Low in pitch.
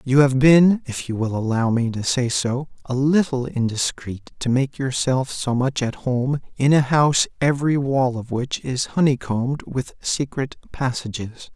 Yes: low, 130 Hz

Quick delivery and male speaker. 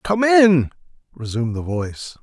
No: slow, 135 wpm; male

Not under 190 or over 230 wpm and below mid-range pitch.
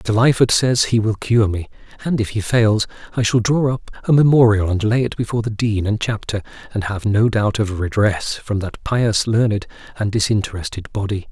Yes: average, 200 wpm; low, 110 Hz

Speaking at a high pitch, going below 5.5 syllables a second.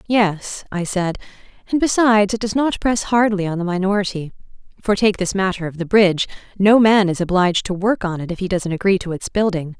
No: high, 195 Hz; 5.8 syllables/s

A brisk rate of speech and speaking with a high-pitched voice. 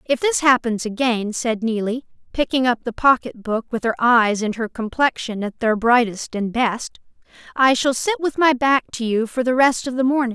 Yes: fast, 210 wpm; high, 245 Hz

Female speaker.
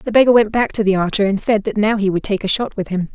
Yes: female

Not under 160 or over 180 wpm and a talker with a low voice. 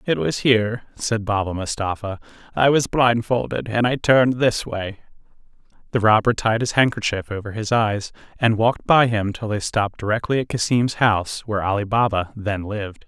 Yes: average, 175 wpm; low, 110 Hz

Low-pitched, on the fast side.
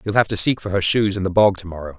Yes: very low, 95 Hz; fast, 360 wpm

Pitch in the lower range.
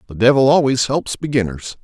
Yes: low, 125 Hz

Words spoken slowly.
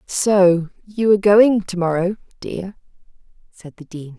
Yes: slow, 130 wpm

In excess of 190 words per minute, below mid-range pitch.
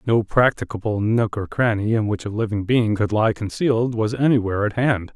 Yes: average, 200 wpm; low, 110 Hz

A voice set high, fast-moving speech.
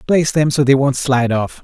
No: low, 135 Hz; fast, 255 wpm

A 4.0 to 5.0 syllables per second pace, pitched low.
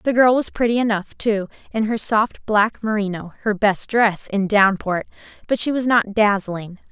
No: 4.6 syllables/s; high, 210 Hz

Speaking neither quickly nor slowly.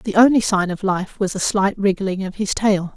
No: fast, 245 wpm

